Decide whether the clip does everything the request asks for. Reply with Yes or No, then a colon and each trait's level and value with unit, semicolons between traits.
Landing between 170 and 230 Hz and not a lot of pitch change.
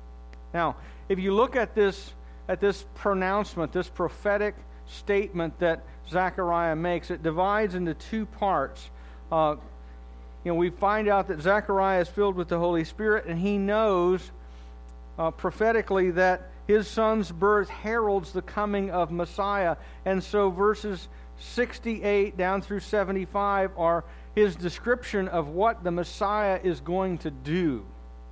No: medium, 185 Hz; average, 3.7 semitones